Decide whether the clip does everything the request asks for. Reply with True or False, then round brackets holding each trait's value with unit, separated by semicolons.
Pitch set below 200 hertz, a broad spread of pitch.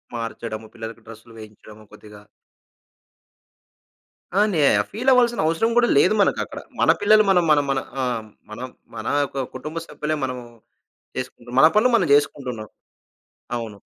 True (135 Hz; 7.8 semitones)